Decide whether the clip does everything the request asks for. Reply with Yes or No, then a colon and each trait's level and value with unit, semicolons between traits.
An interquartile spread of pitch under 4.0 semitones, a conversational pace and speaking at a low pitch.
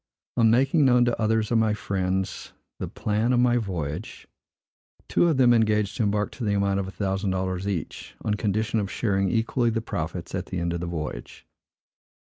Yes: average, 3.3 semitones; average, 195 wpm; low, 105 Hz